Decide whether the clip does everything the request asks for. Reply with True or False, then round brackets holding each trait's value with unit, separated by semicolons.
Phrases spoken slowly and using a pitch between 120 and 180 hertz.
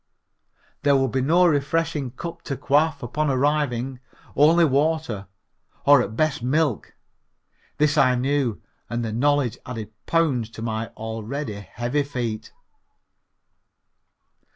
True (120 wpm; 135 Hz)